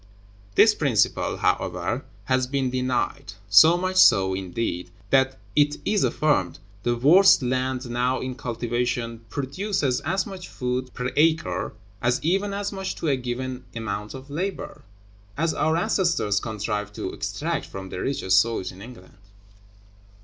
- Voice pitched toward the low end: Yes, low, 130 Hz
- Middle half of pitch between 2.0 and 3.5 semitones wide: No, wide, 5.4 semitones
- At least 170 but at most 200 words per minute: No, average, 140 wpm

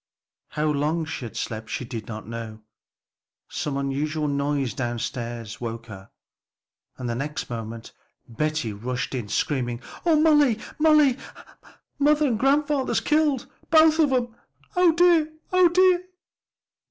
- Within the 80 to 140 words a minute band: Yes, slow, 135 wpm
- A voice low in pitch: No, medium, 150 Hz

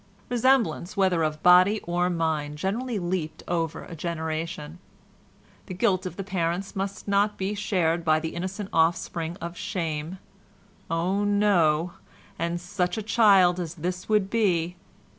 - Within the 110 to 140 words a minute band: Yes, slow, 135 wpm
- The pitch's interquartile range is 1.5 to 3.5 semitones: Yes, average, 3.1 semitones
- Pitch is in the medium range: Yes, medium, 180 Hz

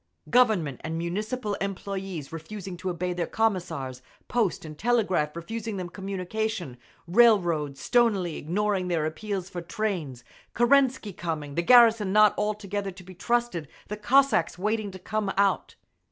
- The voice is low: No, high, 195 Hz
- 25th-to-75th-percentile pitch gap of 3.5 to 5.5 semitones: Yes, average, 4.1 semitones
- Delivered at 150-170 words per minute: No, average, 140 wpm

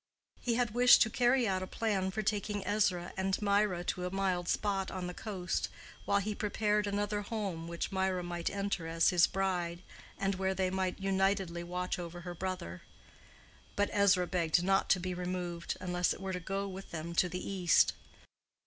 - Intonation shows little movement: Yes, narrow, 2.1 semitones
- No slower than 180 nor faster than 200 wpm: Yes, average, 185 wpm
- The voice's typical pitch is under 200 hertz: Yes, high, 190 Hz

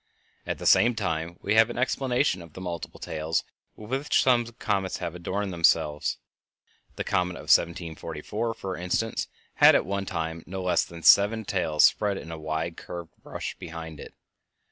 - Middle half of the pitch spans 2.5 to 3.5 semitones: No, average, 4.4 semitones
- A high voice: No, very low, 90 Hz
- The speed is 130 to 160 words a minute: No, average, 170 wpm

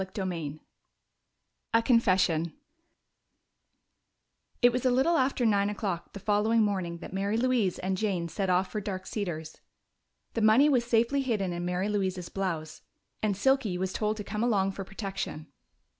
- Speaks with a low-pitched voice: No, high, 200 Hz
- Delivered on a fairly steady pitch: No, average, 3.7 semitones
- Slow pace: No, average, 160 wpm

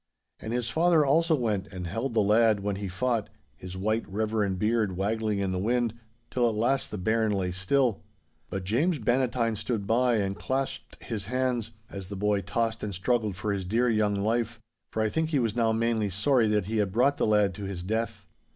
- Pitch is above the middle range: No, low, 110 Hz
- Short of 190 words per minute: No, fast, 205 wpm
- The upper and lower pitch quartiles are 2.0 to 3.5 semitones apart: Yes, average, 3.1 semitones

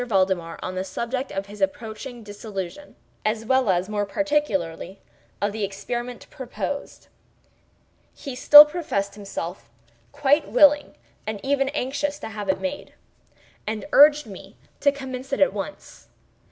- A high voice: Yes, high, 230 Hz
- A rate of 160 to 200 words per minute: No, average, 140 wpm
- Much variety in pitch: Yes, wide, 6.2 semitones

